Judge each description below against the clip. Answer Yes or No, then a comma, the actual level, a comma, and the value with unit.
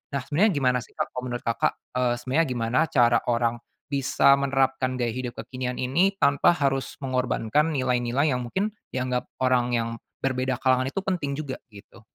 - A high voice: No, low, 130 Hz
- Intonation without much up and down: Yes, narrow, 2.1 semitones